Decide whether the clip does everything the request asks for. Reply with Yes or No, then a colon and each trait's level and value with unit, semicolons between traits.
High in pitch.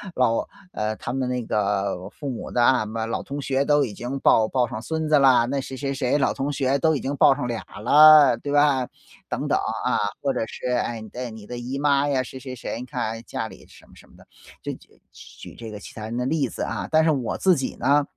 No: low, 130 Hz